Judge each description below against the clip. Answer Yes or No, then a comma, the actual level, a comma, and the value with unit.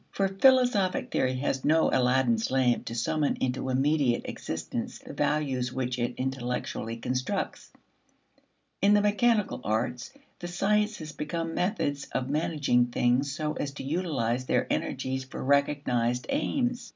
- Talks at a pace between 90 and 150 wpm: Yes, slow, 135 wpm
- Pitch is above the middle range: No, medium, 140 Hz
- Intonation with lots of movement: Yes, wide, 5.7 semitones